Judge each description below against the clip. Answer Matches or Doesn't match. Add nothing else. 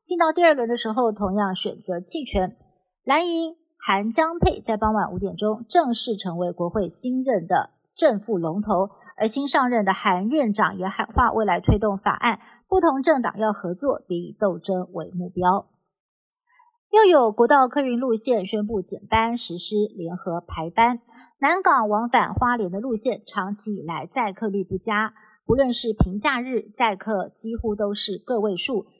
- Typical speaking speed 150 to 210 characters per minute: Doesn't match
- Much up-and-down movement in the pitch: Doesn't match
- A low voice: Doesn't match